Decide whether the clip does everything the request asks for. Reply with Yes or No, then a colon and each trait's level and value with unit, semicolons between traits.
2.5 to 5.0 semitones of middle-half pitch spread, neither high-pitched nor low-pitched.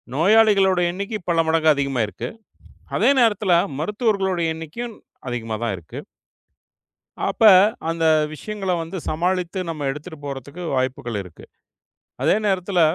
No: wide, 5.6 semitones; medium, 170 Hz